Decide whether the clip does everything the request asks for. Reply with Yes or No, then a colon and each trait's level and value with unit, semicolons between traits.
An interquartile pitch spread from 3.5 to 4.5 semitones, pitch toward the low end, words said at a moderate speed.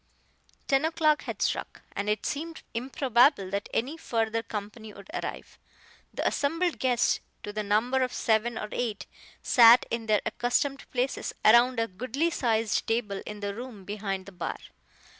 No: average, 3.8 semitones; high, 230 Hz; average, 160 wpm